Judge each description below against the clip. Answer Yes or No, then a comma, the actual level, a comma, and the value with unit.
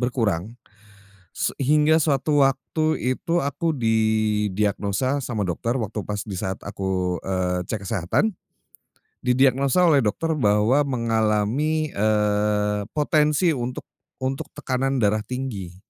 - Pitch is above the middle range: No, low, 115 Hz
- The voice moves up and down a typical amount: Yes, average, 5.0 semitones